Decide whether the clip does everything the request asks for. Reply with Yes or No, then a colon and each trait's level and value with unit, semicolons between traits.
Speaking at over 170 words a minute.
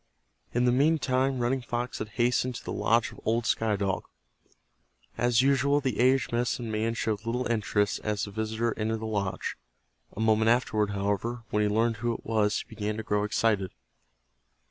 Yes: average, 180 wpm